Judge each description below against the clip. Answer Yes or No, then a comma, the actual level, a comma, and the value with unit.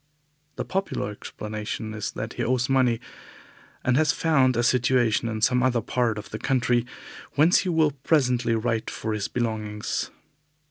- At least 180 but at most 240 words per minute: No, average, 155 wpm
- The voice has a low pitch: Yes, low, 120 Hz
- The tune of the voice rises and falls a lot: No, average, 3.0 semitones